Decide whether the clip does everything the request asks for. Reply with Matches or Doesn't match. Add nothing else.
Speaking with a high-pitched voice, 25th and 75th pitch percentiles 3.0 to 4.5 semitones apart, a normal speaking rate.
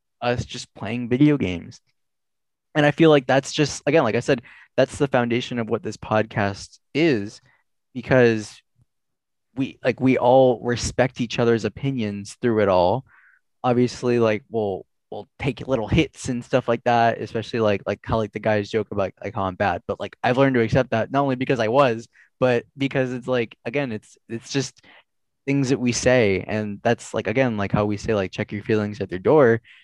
Doesn't match